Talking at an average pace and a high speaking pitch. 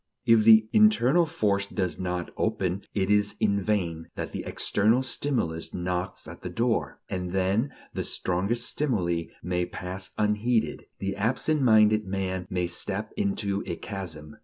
No: average, 150 wpm; low, 100 Hz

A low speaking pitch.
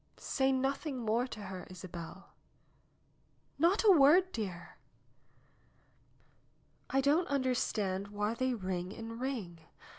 No: high, 230 Hz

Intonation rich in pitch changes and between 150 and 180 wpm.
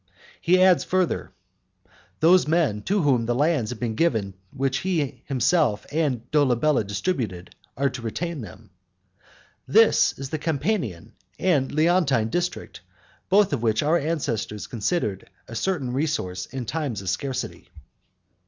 No: wide, 6.5 semitones; slow, 135 wpm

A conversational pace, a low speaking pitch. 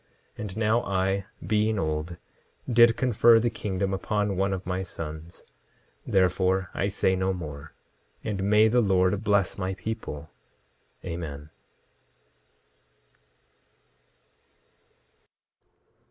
No: slow, 105 wpm; very low, 95 Hz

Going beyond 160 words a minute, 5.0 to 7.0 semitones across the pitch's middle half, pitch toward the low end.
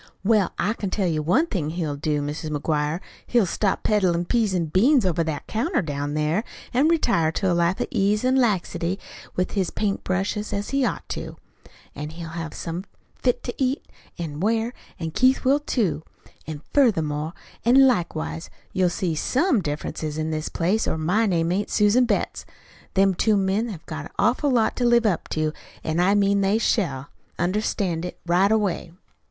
No: average, 185 wpm; wide, 5.4 semitones; medium, 185 Hz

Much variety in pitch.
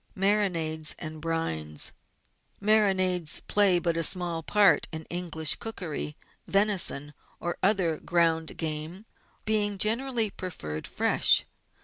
No: average, 4.1 semitones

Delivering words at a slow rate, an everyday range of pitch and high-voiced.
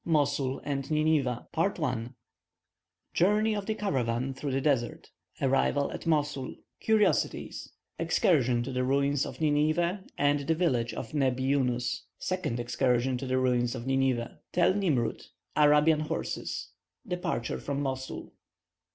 No: slow, 125 wpm; average, 3.4 semitones; medium, 140 Hz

